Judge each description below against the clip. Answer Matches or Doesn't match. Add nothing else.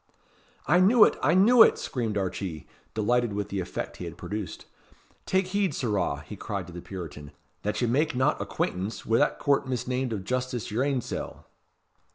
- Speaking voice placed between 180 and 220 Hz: Doesn't match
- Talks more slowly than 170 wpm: Doesn't match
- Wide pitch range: Matches